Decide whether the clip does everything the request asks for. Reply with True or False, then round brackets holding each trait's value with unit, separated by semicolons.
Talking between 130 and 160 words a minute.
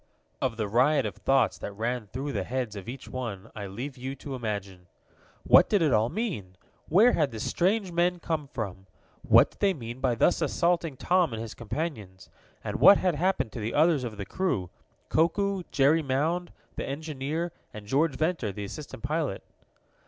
False (185 wpm)